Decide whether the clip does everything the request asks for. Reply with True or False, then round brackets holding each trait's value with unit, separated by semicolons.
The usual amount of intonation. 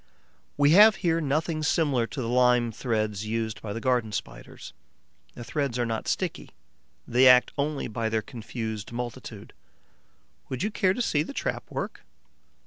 True (4.8 semitones)